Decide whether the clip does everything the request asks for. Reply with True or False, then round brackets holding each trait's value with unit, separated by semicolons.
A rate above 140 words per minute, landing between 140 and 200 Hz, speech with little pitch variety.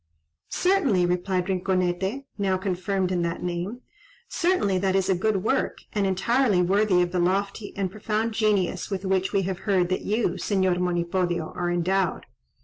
True (160 wpm; 190 Hz; 2.2 semitones)